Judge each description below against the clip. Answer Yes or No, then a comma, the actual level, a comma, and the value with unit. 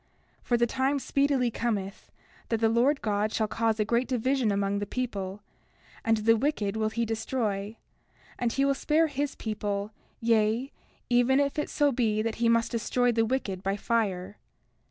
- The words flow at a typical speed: Yes, average, 175 wpm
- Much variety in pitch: No, average, 3.3 semitones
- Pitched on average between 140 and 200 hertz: No, high, 230 Hz